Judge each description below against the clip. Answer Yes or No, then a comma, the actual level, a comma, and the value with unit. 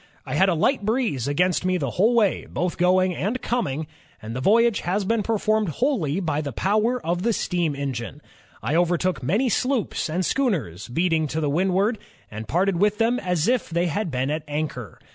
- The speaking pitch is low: No, medium, 180 Hz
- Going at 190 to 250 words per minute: Yes, average, 200 wpm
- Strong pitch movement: Yes, wide, 6.0 semitones